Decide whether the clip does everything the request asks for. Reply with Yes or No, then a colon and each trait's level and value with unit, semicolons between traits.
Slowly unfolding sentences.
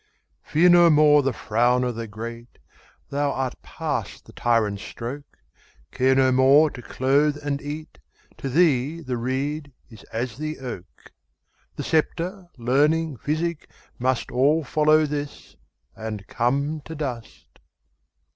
Yes: slow, 120 wpm